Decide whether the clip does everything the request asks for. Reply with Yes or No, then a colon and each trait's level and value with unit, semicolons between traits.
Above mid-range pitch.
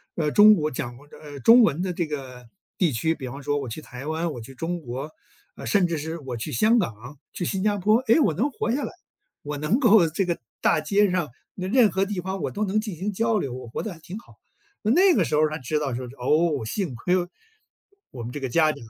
No: medium, 160 Hz